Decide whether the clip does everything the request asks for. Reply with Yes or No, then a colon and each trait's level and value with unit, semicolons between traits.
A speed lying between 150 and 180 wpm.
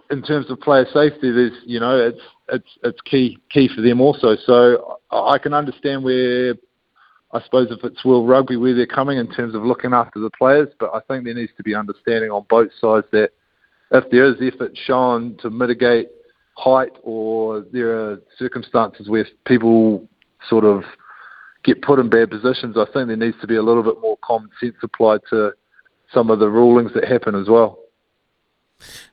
No: average, 190 wpm